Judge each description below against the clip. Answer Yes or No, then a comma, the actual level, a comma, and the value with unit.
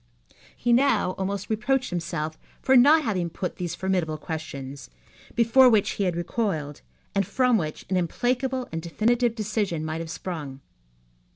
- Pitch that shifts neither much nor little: No, wide, 6.7 semitones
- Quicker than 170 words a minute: No, average, 150 wpm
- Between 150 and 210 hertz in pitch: Yes, high, 190 Hz